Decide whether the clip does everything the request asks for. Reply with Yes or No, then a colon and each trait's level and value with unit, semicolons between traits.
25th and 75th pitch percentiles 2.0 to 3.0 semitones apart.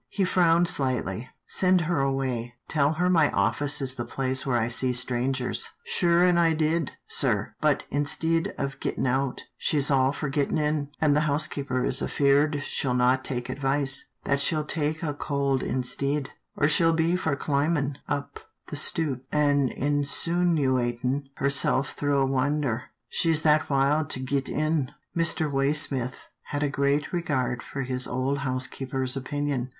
Yes: average, 2.7 semitones